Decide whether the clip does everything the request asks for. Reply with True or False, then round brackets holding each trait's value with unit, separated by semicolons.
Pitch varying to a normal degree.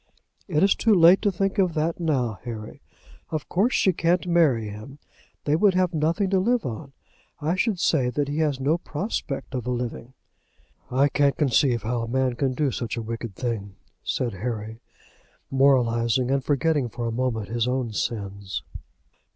False (5.8 semitones)